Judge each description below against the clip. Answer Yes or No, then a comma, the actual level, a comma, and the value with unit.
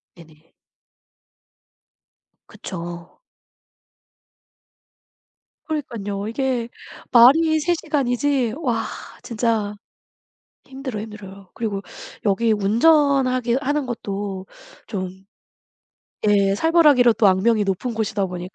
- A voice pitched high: Yes, high, 225 Hz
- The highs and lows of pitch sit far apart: No, average, 5.0 semitones